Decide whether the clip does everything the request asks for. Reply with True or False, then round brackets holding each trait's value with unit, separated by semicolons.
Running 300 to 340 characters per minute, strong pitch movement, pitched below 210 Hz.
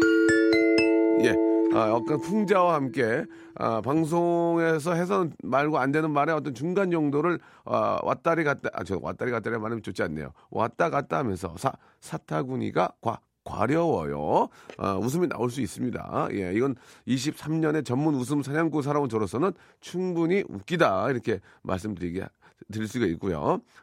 True (315 characters per minute; 6.9 semitones; 140 Hz)